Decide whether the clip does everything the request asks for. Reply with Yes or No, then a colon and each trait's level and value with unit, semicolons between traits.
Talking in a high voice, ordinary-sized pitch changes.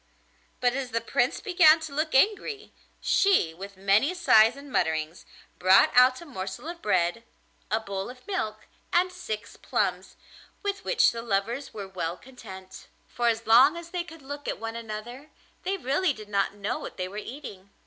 No: high, 235 Hz; wide, 7.5 semitones